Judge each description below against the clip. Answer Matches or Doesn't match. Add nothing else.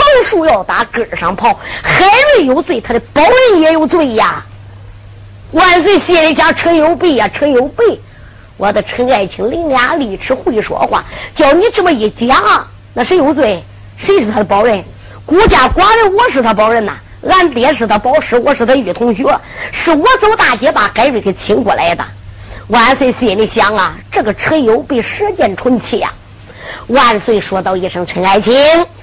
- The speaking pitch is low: Doesn't match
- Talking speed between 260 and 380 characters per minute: Doesn't match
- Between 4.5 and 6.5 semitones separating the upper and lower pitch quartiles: Doesn't match